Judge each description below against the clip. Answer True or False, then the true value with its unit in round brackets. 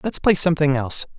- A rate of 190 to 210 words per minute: True (200 wpm)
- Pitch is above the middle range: False (155 Hz)